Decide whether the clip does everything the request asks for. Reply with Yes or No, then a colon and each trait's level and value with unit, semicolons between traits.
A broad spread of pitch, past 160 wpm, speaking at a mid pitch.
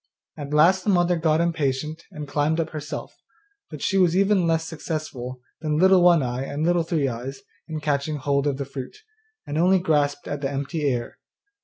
No: average, 3.2 semitones; average, 190 wpm; medium, 155 Hz